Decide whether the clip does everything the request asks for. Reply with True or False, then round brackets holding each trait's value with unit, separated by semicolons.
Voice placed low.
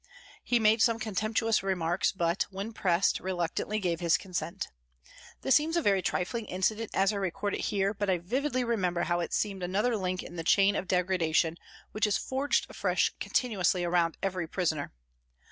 False (195 Hz)